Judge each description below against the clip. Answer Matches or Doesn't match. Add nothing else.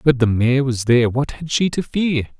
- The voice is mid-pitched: Doesn't match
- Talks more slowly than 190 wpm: Doesn't match